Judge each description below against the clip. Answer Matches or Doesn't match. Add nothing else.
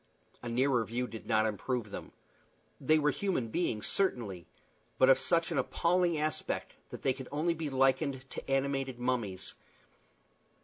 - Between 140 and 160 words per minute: Matches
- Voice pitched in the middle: Doesn't match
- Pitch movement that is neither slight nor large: Matches